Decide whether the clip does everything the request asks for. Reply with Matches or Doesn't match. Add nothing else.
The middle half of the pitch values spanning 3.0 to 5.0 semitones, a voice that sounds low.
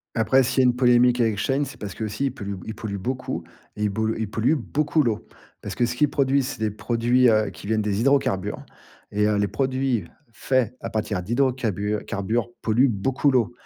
Matches